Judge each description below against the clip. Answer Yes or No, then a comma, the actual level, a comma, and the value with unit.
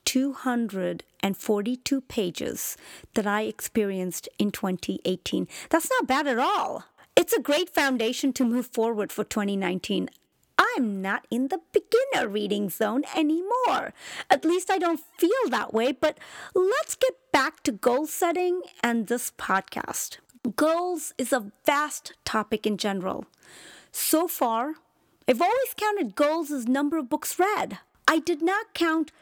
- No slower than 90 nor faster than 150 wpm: Yes, average, 140 wpm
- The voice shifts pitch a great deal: Yes, wide, 7.4 semitones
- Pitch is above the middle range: Yes, very high, 270 Hz